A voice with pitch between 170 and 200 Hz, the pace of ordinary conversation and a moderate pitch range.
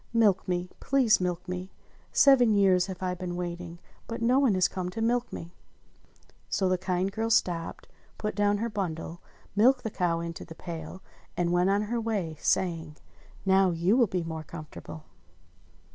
Yes: medium, 185 Hz; average, 175 wpm; average, 3.5 semitones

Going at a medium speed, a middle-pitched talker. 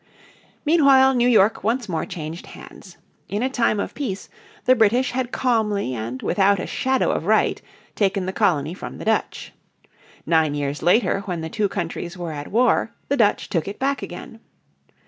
No: average, 175 wpm; high, 200 Hz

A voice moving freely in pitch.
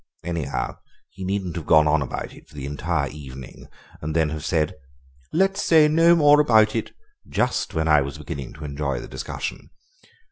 Yes: wide, 7.2 semitones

